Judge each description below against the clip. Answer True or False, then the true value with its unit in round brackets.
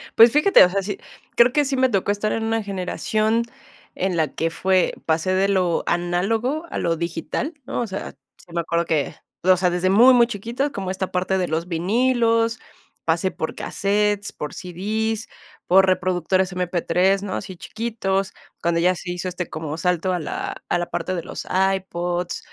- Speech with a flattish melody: False (3.7 semitones)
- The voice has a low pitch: False (190 Hz)